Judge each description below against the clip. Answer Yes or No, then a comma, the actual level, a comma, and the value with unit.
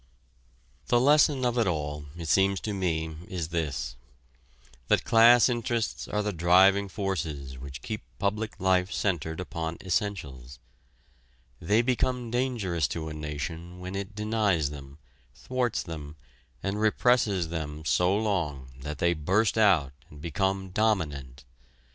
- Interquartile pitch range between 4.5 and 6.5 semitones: Yes, wide, 5.6 semitones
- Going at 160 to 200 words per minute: No, slow, 135 wpm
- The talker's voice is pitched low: Yes, very low, 90 Hz